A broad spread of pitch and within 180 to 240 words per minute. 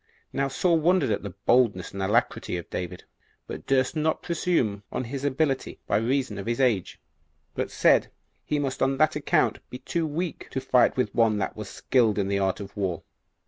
Yes: wide, 5.8 semitones; average, 200 wpm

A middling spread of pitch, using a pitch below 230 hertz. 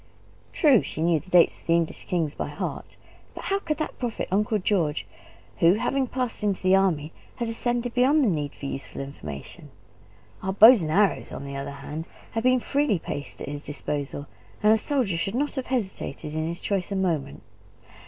No: wide, 7.6 semitones; high, 190 Hz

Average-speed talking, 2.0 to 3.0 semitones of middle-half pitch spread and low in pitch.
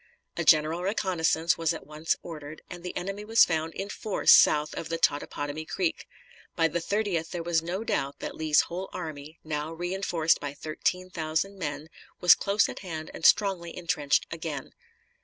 No: average, 175 wpm; average, 2.7 semitones; medium, 165 Hz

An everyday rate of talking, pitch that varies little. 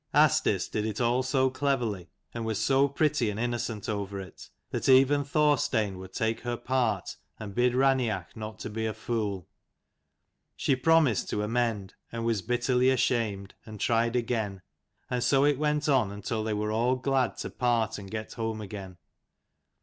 No: average, 170 wpm; average, 3.6 semitones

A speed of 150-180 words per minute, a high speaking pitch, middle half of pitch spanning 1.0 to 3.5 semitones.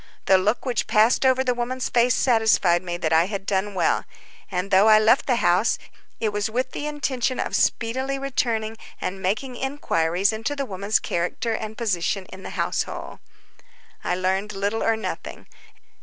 No: average, 170 wpm; high, 220 Hz; average, 4.5 semitones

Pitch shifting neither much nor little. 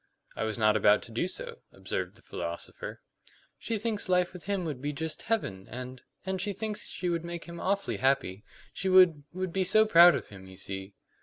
No: wide, 7.7 semitones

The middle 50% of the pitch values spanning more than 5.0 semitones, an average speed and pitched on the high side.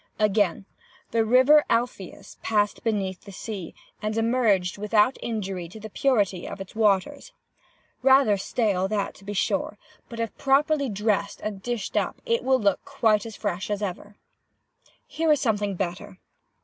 No: average, 3.4 semitones; average, 150 wpm; high, 215 Hz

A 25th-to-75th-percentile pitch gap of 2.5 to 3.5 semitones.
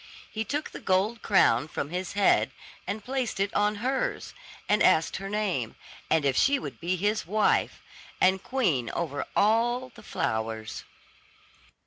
No: wide, 5.6 semitones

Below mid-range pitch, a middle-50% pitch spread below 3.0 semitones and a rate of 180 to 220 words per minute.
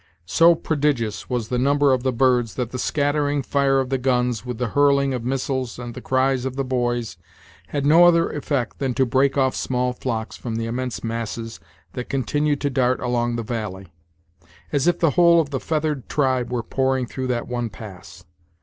Yes: low, 130 Hz; narrow, 2.6 semitones; average, 195 wpm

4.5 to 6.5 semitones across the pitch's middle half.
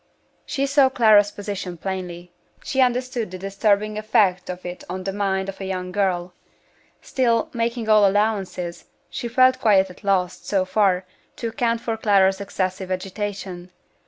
No: average, 3.1 semitones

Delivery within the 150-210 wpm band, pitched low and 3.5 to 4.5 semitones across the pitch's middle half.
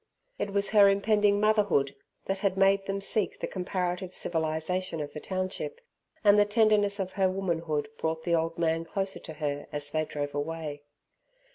No: average, 165 wpm; medium, 185 Hz; average, 3.8 semitones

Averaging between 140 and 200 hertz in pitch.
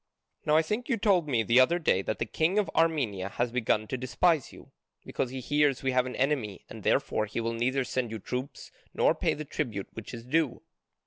No: low, 130 Hz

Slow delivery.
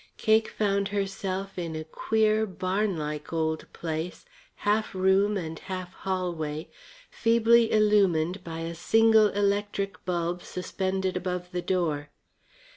Yes: slow, 115 wpm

